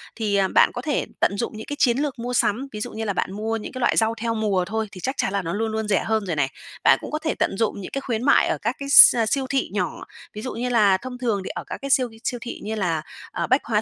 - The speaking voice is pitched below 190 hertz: No, high, 225 Hz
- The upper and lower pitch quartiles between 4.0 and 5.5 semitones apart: No, average, 3.5 semitones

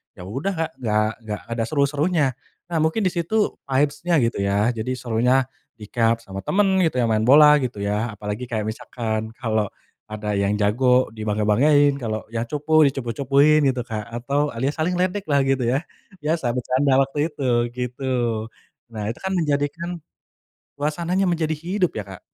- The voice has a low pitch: Yes, low, 130 Hz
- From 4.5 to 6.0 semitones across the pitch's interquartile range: Yes, wide, 5.4 semitones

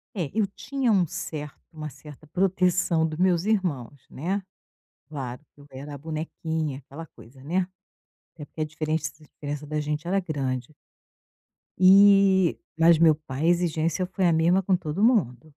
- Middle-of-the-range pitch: Yes, medium, 160 Hz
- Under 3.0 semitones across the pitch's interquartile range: No, average, 3.7 semitones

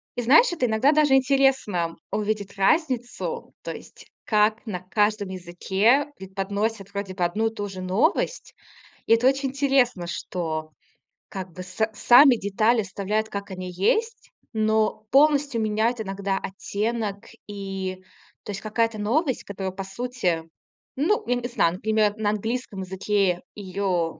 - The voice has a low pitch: No, high, 210 Hz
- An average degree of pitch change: Yes, average, 4.1 semitones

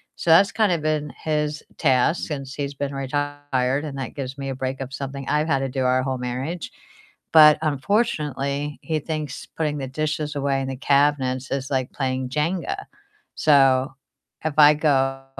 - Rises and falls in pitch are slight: Yes, narrow, 2.2 semitones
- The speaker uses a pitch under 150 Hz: Yes, medium, 140 Hz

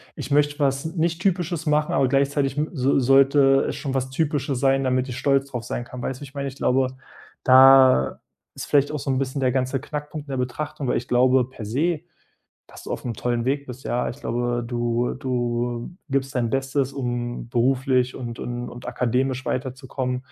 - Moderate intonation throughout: No, narrow, 2.1 semitones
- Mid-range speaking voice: No, low, 130 Hz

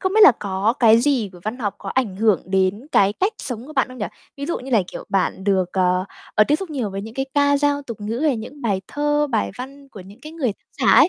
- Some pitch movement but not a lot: No, wide, 6.0 semitones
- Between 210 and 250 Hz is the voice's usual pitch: Yes, high, 235 Hz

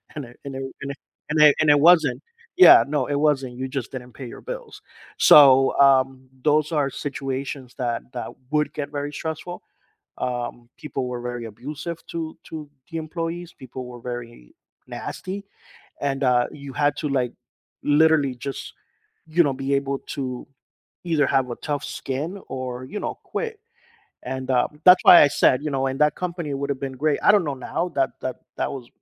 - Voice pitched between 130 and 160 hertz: Yes, medium, 140 Hz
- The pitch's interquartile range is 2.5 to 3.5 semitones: Yes, average, 3.0 semitones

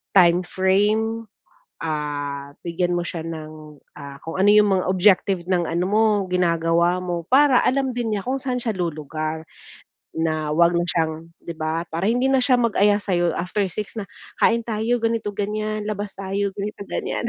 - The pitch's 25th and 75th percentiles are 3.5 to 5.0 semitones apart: Yes, average, 4.4 semitones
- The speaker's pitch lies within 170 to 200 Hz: Yes, medium, 185 Hz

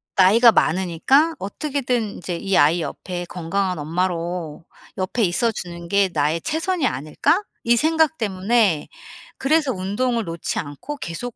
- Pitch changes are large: Yes, wide, 6.3 semitones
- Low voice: No, high, 195 Hz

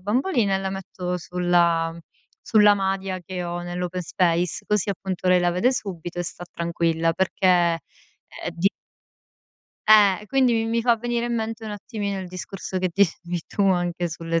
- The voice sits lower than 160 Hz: No, medium, 185 Hz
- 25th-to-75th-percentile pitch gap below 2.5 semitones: No, average, 2.9 semitones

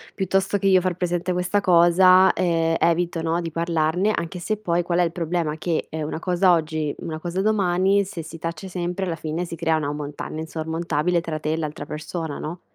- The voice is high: No, medium, 170 Hz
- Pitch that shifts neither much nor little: No, narrow, 2.1 semitones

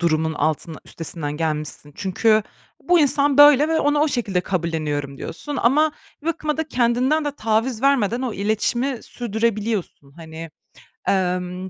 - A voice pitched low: No, high, 220 Hz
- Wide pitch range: Yes, wide, 8.8 semitones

